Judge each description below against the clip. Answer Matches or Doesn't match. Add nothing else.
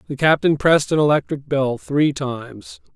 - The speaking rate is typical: Matches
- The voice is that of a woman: Doesn't match